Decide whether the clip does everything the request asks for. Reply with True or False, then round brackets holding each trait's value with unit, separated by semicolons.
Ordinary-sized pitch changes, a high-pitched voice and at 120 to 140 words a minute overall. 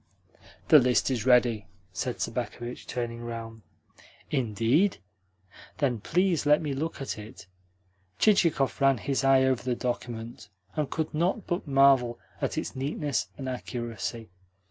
False (3.5 semitones; 130 Hz; 135 wpm)